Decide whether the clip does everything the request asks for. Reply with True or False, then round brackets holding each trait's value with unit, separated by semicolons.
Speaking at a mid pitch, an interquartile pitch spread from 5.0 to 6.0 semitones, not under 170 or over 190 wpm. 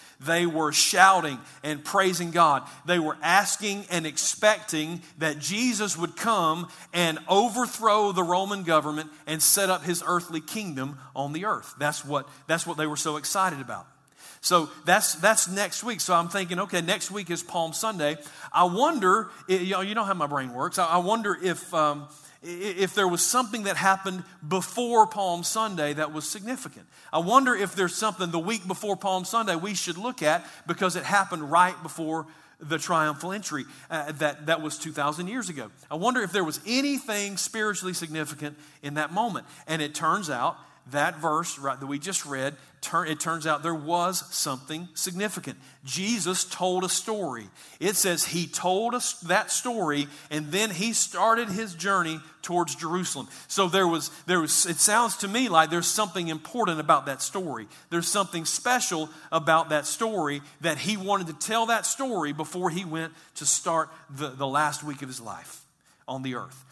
False (175 Hz; 4.4 semitones; 180 wpm)